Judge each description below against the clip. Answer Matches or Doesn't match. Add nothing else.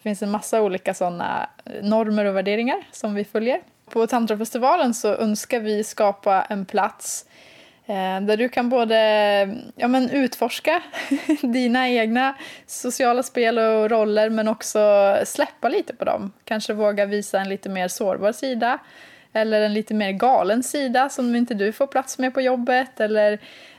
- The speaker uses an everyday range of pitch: Matches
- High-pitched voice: Matches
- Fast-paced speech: Doesn't match